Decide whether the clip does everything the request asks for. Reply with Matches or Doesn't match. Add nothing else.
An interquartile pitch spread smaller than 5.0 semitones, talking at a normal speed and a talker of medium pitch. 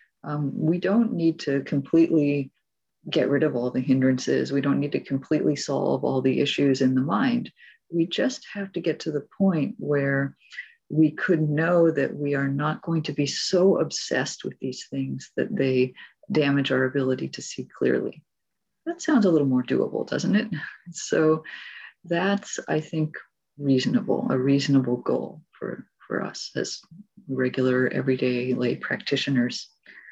Matches